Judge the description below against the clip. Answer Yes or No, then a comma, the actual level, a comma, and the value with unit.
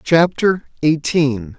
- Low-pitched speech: No, medium, 155 Hz